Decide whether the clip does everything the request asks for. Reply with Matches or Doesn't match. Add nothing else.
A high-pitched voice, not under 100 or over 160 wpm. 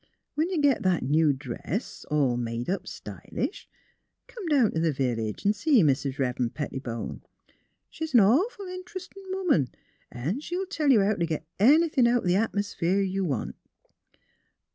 Matches